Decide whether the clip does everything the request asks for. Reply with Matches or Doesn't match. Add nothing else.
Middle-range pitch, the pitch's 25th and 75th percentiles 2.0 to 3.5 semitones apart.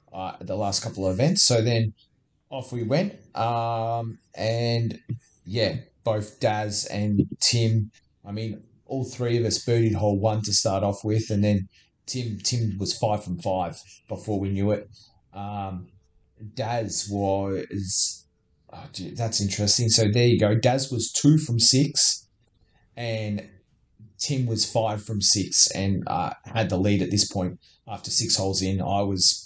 Doesn't match